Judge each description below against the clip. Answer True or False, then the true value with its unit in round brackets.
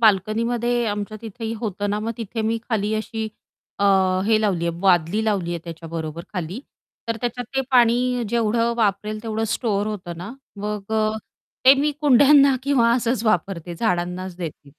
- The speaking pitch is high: True (215 Hz)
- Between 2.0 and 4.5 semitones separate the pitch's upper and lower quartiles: True (3.7 semitones)